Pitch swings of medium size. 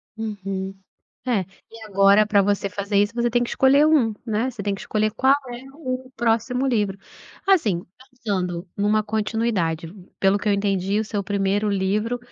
Yes: average, 3.2 semitones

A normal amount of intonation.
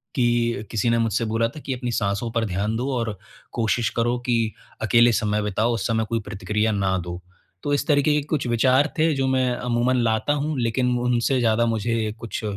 No: narrow, 2.2 semitones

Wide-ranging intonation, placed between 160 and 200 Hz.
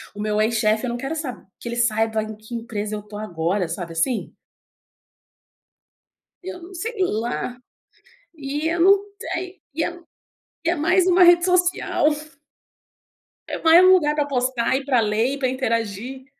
No: wide, 7.4 semitones; very high, 255 Hz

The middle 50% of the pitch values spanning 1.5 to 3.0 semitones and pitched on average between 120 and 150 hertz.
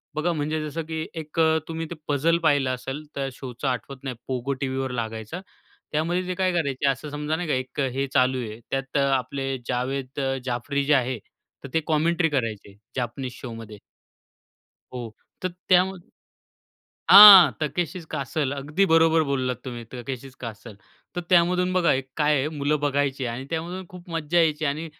No: average, 4.0 semitones; medium, 140 Hz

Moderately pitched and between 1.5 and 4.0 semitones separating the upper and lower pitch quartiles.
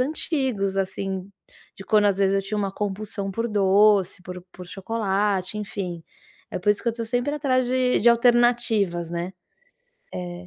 No: high, 205 Hz; average, 3.6 semitones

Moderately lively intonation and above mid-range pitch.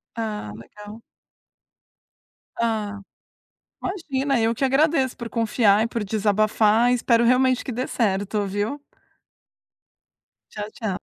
Yes: average, 3.2 semitones; high, 225 Hz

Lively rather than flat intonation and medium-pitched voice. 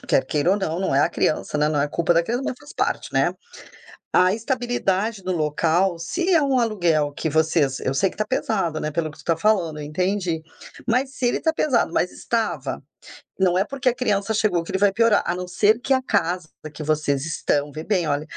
Yes: wide, 6.0 semitones; medium, 180 Hz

